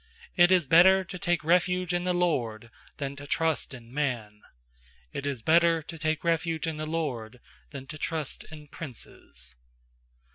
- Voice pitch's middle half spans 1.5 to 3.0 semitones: No, average, 4.3 semitones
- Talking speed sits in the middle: Yes, average, 160 wpm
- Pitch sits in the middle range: Yes, medium, 155 Hz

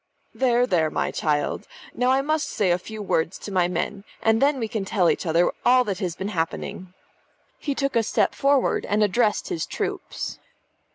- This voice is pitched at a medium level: No, high, 210 Hz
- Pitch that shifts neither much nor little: No, wide, 5.7 semitones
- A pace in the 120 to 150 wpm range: No, average, 195 wpm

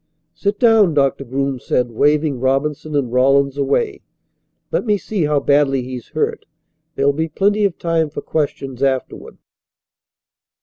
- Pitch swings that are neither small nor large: Yes, average, 3.3 semitones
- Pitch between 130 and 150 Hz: Yes, medium, 140 Hz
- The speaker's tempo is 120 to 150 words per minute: Yes, average, 140 wpm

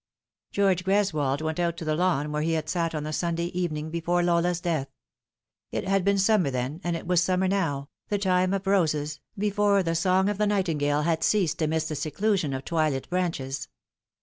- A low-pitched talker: No, medium, 170 Hz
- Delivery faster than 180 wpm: Yes, average, 190 wpm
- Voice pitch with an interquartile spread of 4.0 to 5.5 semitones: No, average, 3.6 semitones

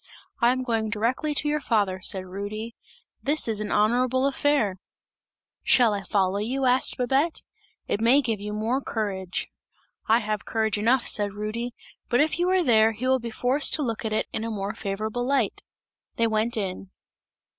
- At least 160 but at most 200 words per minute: Yes, average, 180 wpm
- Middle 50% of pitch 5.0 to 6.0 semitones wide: No, average, 3.6 semitones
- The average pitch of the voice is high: Yes, high, 225 Hz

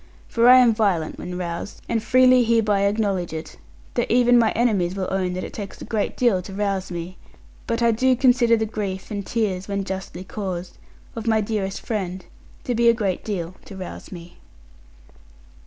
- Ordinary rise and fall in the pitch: Yes, average, 3.7 semitones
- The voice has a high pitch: Yes, high, 205 Hz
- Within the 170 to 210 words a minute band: Yes, average, 190 wpm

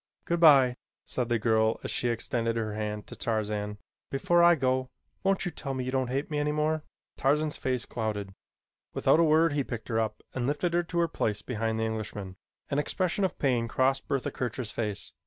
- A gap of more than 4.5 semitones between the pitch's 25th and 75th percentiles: Yes, average, 5.1 semitones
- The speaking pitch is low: Yes, low, 130 Hz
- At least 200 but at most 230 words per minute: Yes, fast, 205 wpm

